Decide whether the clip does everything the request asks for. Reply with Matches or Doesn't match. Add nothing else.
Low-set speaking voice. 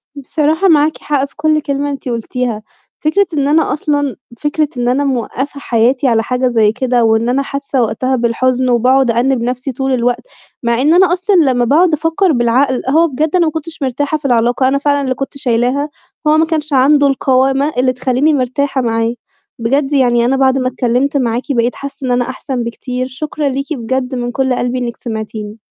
Doesn't match